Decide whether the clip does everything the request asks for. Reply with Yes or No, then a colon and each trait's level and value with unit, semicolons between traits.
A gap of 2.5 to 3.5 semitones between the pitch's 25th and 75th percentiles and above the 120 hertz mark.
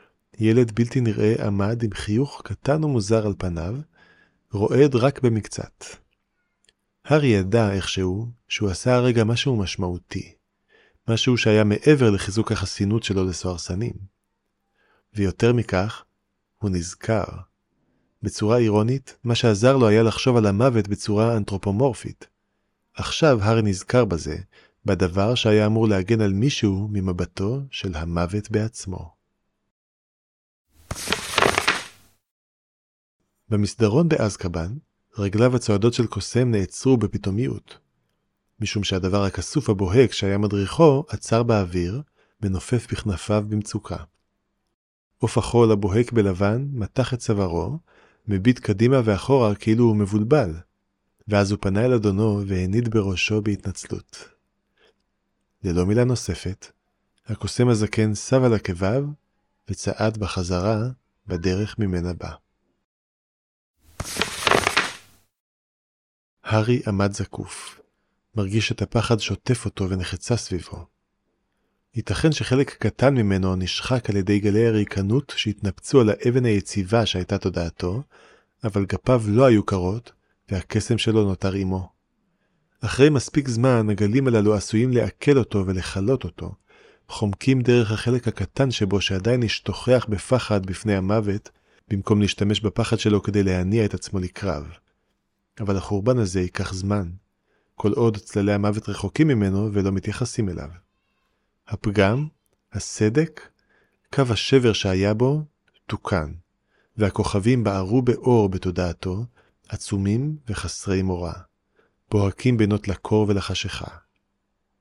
No: average, 3.2 semitones; low, 105 Hz